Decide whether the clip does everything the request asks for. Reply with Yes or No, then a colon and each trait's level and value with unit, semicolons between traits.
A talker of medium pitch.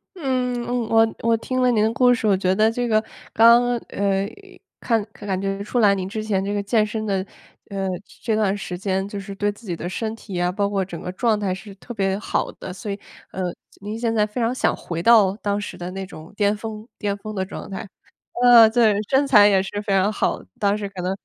No: high, 205 Hz